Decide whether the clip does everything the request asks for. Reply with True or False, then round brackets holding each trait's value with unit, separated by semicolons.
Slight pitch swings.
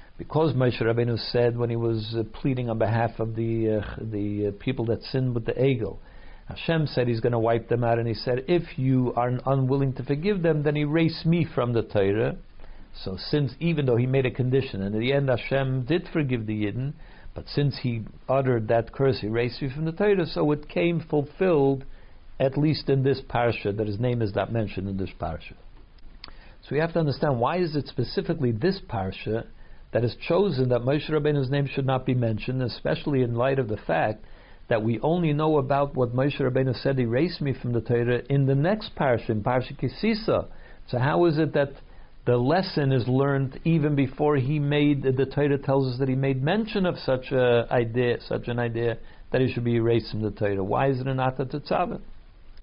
False (3.8 semitones)